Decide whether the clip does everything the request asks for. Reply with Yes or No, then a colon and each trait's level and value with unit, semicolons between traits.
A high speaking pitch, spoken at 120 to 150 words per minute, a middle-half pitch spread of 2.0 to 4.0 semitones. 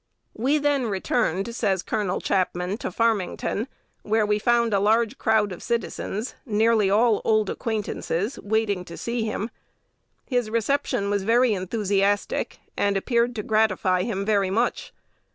Yes: high, 215 Hz; average, 140 wpm; average, 2.7 semitones